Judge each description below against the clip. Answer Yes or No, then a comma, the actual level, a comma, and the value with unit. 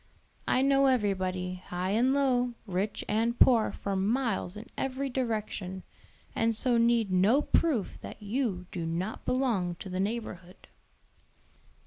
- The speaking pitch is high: Yes, high, 220 Hz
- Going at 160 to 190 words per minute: No, slow, 135 wpm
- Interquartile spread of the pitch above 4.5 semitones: Yes, average, 5.0 semitones